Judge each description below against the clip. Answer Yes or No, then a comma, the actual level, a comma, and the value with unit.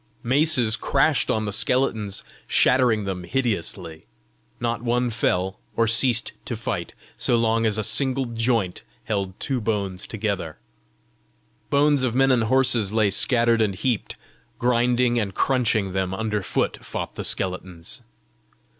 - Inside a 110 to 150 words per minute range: Yes, slow, 135 wpm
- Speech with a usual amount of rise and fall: Yes, average, 3.9 semitones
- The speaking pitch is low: Yes, low, 115 Hz